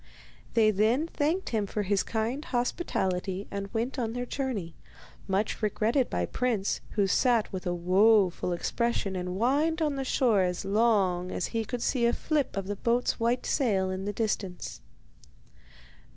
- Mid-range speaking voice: No, high, 220 Hz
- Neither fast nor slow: Yes, average, 165 wpm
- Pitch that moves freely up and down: No, average, 4.3 semitones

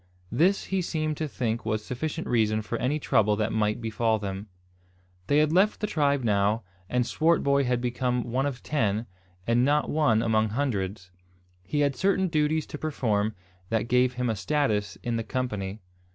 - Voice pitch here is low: Yes, low, 125 Hz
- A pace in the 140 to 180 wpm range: Yes, average, 175 wpm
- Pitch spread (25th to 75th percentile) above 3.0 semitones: Yes, average, 5.2 semitones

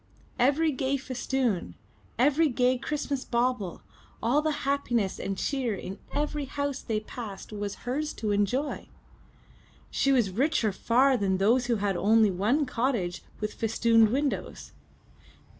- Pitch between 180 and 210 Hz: No, high, 245 Hz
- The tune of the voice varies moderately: Yes, average, 4.7 semitones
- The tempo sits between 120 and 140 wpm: Yes, slow, 135 wpm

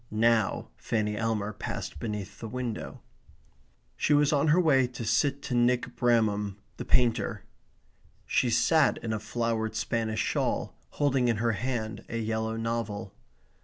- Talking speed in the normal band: Yes, average, 145 wpm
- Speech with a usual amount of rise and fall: No, narrow, 2.3 semitones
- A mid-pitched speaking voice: No, low, 115 Hz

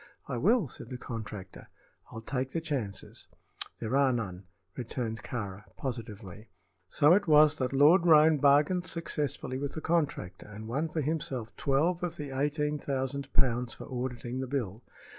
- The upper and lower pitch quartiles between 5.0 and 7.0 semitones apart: No, average, 4.5 semitones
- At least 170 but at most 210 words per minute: No, average, 160 wpm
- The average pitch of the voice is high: No, low, 135 Hz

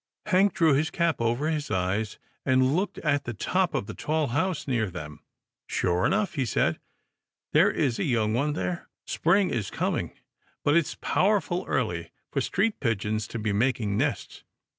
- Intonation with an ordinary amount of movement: No, wide, 7.3 semitones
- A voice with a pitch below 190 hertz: Yes, low, 135 Hz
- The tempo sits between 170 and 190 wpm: Yes, average, 180 wpm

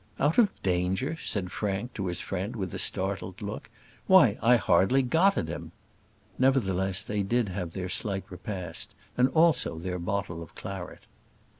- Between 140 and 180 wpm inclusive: Yes, average, 160 wpm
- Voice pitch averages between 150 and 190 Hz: No, very low, 95 Hz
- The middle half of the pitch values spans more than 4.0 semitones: Yes, average, 4.9 semitones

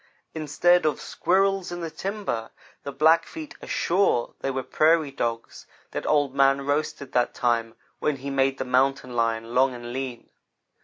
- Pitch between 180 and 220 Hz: No, low, 135 Hz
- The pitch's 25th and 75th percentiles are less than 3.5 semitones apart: No, average, 4.4 semitones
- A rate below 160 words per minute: No, average, 165 wpm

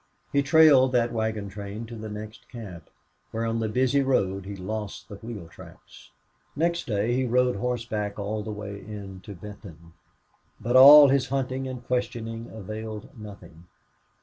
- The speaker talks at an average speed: Yes, average, 160 wpm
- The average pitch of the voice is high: No, low, 110 Hz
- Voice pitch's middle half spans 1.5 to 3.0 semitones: No, average, 3.6 semitones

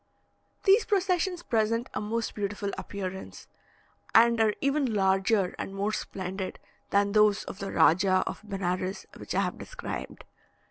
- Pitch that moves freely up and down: No, average, 3.3 semitones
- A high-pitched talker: Yes, high, 205 Hz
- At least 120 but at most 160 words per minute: Yes, average, 140 wpm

